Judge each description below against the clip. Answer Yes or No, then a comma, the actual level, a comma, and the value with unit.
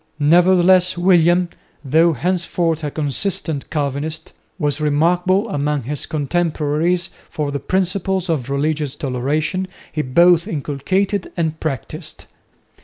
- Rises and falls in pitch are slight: No, average, 3.5 semitones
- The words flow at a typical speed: No, slow, 110 wpm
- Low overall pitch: No, medium, 160 Hz